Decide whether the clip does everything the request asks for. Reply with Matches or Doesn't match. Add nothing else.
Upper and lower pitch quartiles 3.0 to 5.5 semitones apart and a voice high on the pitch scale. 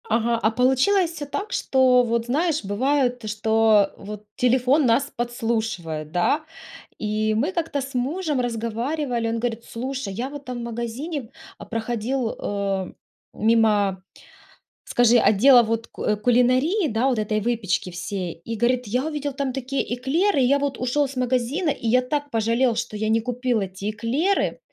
Matches